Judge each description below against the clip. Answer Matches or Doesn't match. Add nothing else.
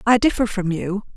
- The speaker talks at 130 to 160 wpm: Doesn't match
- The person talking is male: Doesn't match